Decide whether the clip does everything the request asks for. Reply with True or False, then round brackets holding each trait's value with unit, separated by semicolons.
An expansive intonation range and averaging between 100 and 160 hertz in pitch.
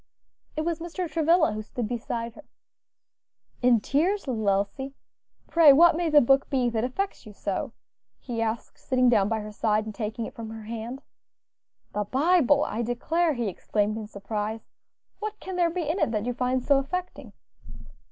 False (6.2 semitones; 245 Hz)